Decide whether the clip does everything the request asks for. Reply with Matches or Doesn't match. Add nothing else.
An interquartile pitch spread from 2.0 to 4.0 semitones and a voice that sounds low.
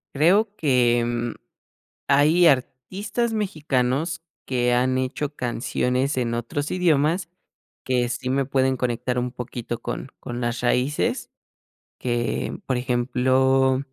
Matches